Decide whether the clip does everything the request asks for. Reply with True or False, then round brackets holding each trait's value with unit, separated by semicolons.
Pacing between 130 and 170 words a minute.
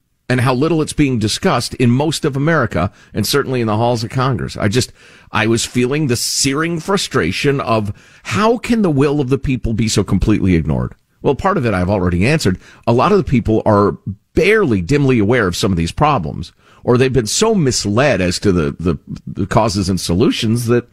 False (205 wpm)